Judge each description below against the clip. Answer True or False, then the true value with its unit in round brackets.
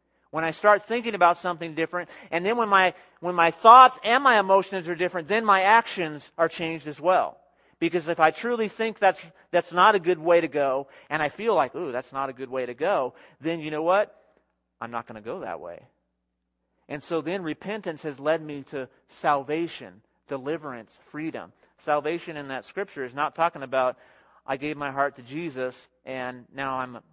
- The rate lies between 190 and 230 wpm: True (195 wpm)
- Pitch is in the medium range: True (165 Hz)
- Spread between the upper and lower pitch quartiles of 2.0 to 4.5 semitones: False (5.0 semitones)